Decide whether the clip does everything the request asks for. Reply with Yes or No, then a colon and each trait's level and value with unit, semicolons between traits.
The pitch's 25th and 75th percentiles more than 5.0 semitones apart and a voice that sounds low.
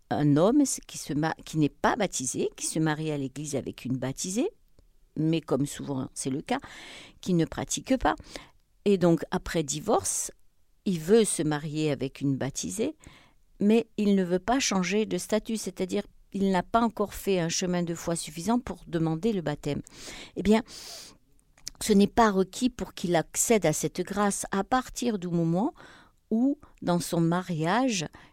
No: wide, 5.5 semitones; medium, 180 Hz